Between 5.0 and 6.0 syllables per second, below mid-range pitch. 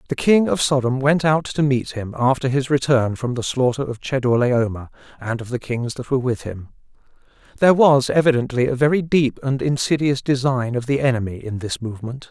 Yes: 5.5 syllables/s; low, 130 Hz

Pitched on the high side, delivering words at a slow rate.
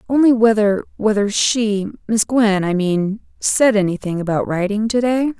Yes: high, 210 Hz; slow, 120 wpm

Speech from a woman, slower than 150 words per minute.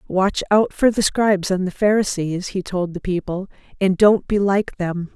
No: female; average, 200 wpm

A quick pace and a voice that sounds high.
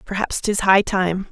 No: average, 180 wpm; high, 195 Hz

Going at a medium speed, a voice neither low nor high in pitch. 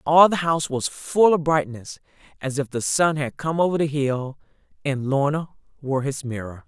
Yes: average, 190 wpm; medium, 145 Hz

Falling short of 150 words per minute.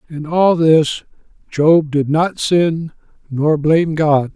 Yes: average, 140 wpm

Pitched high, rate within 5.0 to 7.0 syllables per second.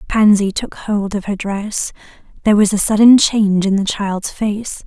No: high, 205 Hz; 4.6 syllables/s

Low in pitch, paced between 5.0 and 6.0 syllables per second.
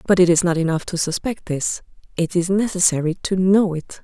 No: medium, 180 Hz; 5.3 syllables/s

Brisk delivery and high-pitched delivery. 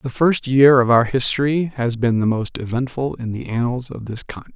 No: fast, 225 wpm; low, 125 Hz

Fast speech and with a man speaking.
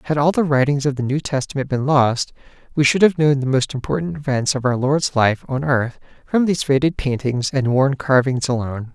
Yes: fast, 215 wpm; male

